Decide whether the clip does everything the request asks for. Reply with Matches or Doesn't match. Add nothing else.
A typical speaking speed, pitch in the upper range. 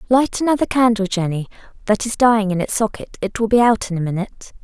Matches